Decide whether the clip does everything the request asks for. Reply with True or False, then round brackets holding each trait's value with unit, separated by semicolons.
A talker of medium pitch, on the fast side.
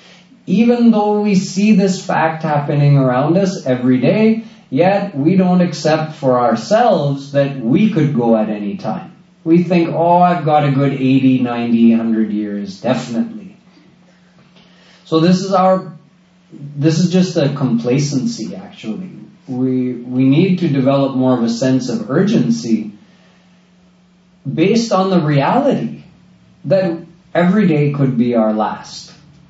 False (165 Hz; 140 wpm)